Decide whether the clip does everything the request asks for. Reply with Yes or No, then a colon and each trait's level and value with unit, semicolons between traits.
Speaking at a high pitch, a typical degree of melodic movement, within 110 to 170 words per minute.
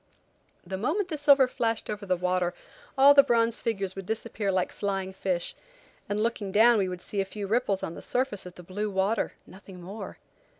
No: high, 200 Hz; average, 3.4 semitones; average, 195 wpm